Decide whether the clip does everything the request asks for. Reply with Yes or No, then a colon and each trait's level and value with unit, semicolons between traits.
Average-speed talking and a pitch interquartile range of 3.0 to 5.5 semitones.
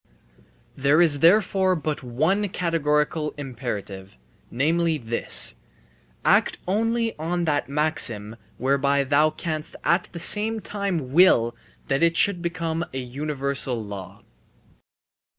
No: slow, 115 wpm; average, 4.5 semitones